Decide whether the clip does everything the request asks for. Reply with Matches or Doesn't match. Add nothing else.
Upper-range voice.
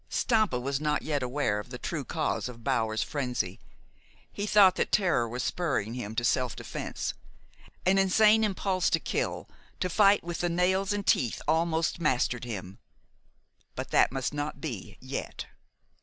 Doesn't match